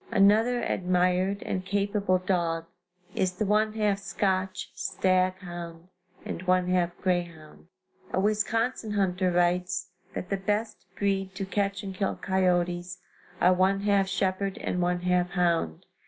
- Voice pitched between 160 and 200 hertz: Yes, medium, 185 Hz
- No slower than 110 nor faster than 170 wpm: Yes, average, 140 wpm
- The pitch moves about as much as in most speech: No, narrow, 1.8 semitones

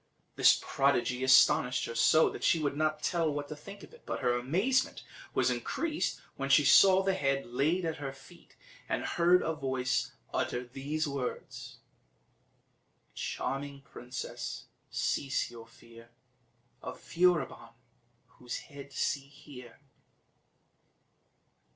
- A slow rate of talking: Yes, slow, 130 wpm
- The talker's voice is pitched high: No, medium, 140 Hz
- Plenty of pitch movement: No, average, 3.9 semitones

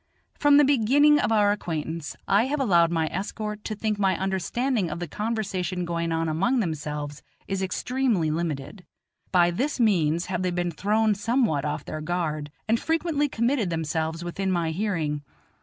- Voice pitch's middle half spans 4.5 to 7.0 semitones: Yes, average, 5.3 semitones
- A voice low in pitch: No, medium, 185 Hz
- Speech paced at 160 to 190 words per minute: Yes, average, 165 wpm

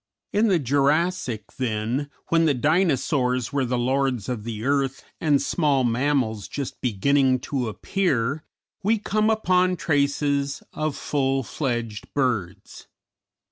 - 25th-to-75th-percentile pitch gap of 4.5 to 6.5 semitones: No, average, 3.7 semitones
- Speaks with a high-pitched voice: No, medium, 140 Hz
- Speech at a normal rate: No, slow, 125 wpm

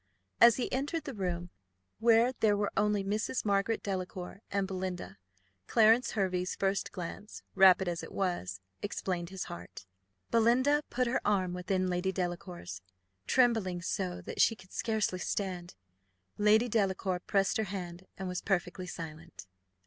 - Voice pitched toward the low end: No, high, 190 Hz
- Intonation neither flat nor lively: Yes, average, 3.3 semitones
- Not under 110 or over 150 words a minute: Yes, average, 145 wpm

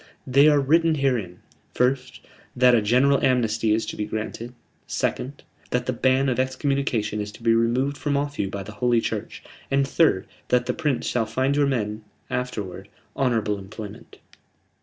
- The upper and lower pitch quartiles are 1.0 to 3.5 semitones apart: No, average, 4.0 semitones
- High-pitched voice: No, low, 125 Hz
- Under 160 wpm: No, average, 170 wpm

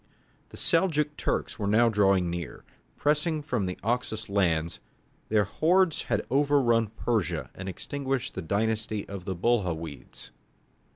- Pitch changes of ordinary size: No, wide, 6.4 semitones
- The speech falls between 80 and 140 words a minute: Yes, slow, 135 wpm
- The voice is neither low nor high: No, low, 110 Hz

